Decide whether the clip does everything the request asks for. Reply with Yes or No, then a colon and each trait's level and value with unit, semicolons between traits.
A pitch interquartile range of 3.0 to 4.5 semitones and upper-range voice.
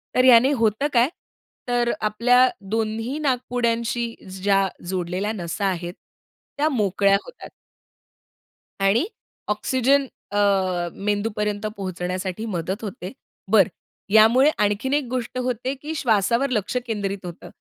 Yes: average, 4.1 semitones; high, 220 Hz